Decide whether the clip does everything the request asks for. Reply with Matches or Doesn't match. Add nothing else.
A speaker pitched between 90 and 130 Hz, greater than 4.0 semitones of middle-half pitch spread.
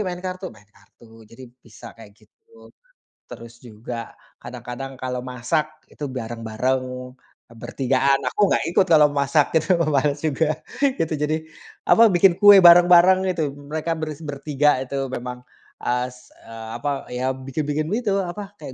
Doesn't match